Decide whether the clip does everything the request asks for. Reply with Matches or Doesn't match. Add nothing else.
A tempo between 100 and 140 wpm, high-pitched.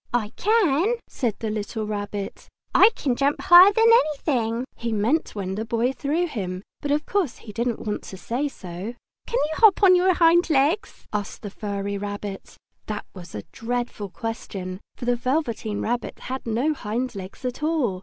Doesn't match